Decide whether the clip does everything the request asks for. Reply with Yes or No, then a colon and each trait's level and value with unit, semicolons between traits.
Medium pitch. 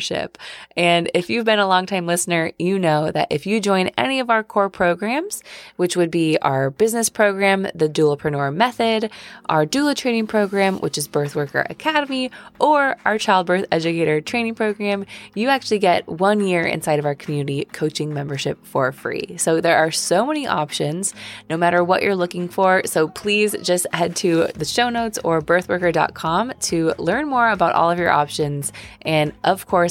Yes: medium, 180 Hz